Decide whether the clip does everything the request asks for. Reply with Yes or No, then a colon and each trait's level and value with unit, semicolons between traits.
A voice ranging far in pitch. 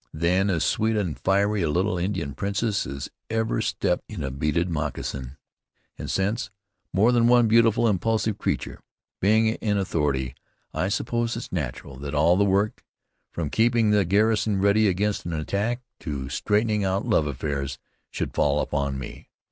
Yes: wide, 6.2 semitones